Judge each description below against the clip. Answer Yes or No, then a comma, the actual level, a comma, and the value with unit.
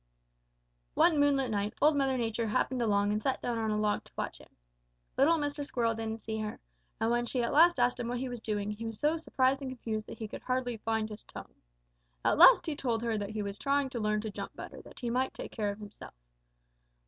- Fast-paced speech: Yes, fast, 245 wpm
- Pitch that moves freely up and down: No, average, 3.5 semitones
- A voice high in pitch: Yes, high, 235 Hz